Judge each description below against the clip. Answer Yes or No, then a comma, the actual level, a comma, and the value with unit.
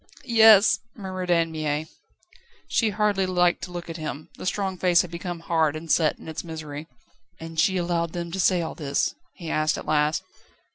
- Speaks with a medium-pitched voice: Yes, medium, 170 Hz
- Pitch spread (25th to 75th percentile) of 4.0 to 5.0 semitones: No, average, 2.8 semitones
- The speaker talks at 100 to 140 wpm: No, average, 190 wpm